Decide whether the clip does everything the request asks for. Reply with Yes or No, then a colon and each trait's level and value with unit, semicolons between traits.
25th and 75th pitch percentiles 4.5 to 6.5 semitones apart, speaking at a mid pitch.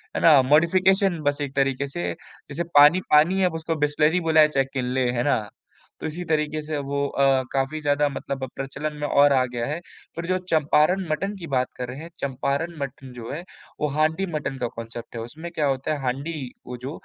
No: average, 2.9 semitones; medium, 145 Hz